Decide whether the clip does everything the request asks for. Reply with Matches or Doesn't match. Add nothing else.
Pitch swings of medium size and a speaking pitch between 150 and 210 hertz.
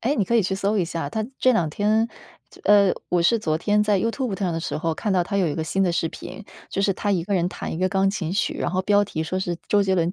Matches